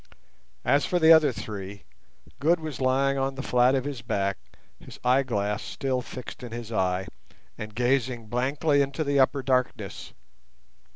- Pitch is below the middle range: Yes, low, 130 Hz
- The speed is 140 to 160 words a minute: Yes, average, 155 wpm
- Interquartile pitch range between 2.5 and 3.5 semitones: Yes, average, 3.1 semitones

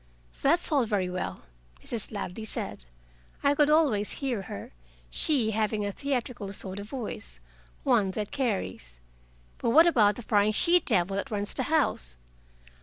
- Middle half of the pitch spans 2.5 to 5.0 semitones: No, wide, 5.6 semitones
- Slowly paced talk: No, average, 155 wpm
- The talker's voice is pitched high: Yes, high, 215 Hz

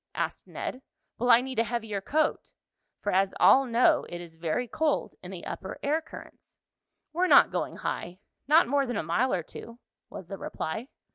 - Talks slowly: No, average, 190 wpm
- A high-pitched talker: Yes, high, 230 Hz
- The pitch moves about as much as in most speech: No, wide, 6.0 semitones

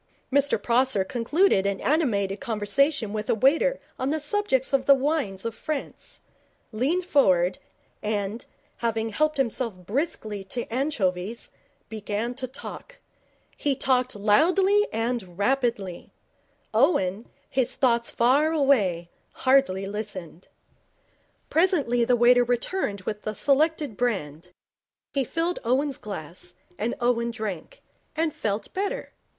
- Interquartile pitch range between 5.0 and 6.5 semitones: Yes, average, 5.3 semitones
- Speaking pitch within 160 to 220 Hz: No, high, 240 Hz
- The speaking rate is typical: No, slow, 120 wpm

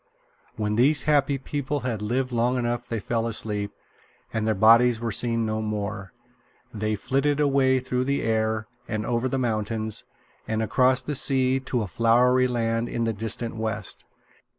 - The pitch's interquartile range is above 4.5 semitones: No, average, 2.8 semitones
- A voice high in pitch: No, low, 115 Hz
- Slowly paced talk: No, average, 165 wpm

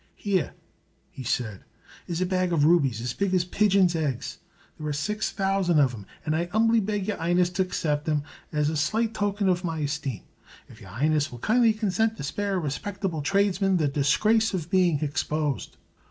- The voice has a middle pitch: Yes, medium, 175 Hz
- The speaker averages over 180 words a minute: Yes, average, 190 wpm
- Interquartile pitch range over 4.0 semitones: Yes, average, 5.0 semitones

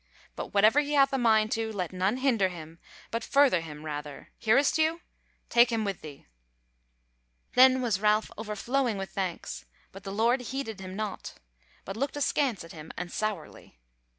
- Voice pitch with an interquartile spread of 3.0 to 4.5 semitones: No, average, 5.3 semitones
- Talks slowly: No, average, 170 wpm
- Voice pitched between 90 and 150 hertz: No, high, 215 Hz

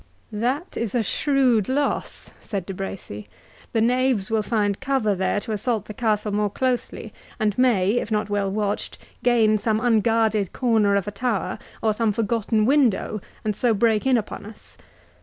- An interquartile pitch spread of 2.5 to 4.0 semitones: Yes, average, 2.8 semitones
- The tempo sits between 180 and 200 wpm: No, average, 170 wpm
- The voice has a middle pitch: No, high, 215 Hz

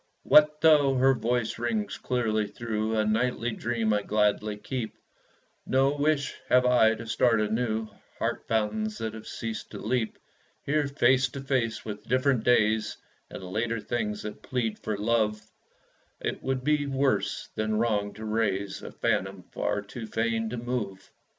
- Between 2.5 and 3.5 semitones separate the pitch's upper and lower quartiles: Yes, average, 3.0 semitones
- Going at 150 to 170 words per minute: Yes, average, 155 wpm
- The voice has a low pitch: Yes, low, 115 Hz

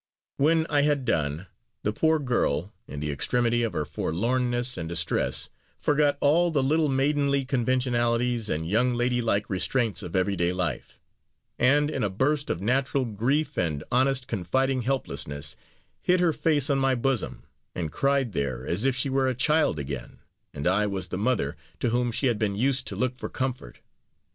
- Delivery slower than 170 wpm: No, average, 175 wpm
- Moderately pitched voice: No, low, 125 Hz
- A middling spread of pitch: No, wide, 5.8 semitones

